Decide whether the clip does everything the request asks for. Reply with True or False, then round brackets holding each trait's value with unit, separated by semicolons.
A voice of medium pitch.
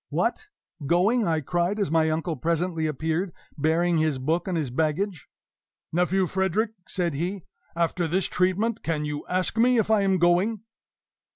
True (175 Hz)